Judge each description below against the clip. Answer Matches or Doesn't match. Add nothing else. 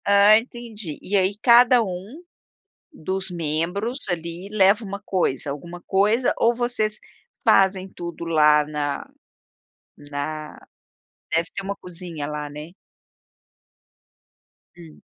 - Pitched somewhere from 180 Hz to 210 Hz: Matches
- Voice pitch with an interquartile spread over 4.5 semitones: Matches